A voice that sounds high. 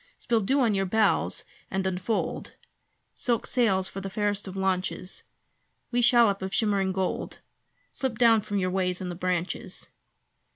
Yes: high, 195 Hz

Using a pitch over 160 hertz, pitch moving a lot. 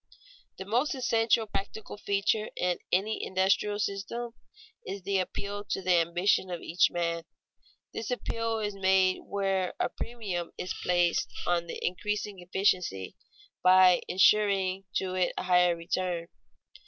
No: high, 190 Hz; narrow, 2.6 semitones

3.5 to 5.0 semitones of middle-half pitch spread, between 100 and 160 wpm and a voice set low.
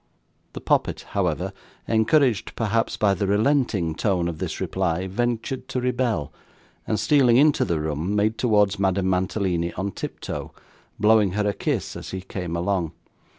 Yes: average, 4.0 semitones; average, 150 wpm; low, 100 Hz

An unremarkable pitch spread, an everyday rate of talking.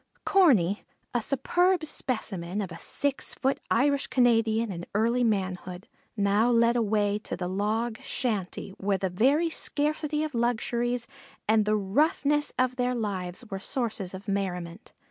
Yes: average, 4.5 semitones; average, 145 wpm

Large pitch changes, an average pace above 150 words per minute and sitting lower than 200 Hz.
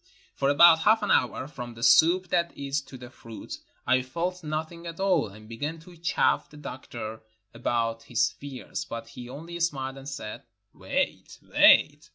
Yes: wide, 5.7 semitones; average, 175 wpm; medium, 140 Hz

